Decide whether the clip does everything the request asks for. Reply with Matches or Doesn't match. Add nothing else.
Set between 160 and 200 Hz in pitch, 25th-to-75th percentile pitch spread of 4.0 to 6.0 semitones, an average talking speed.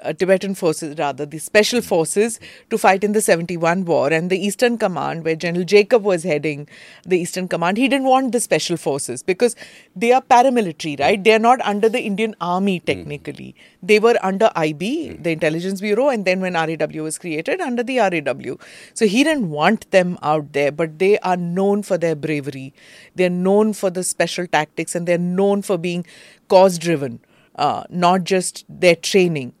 Matches